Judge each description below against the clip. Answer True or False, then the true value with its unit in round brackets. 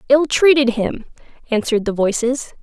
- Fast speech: False (135 wpm)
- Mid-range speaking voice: False (250 Hz)